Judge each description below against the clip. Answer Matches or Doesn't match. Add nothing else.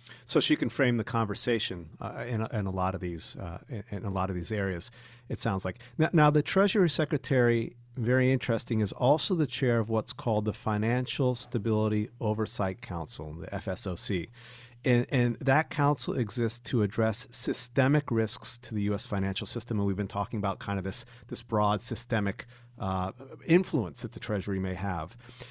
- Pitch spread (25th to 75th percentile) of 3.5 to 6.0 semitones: Matches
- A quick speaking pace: Doesn't match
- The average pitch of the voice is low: Matches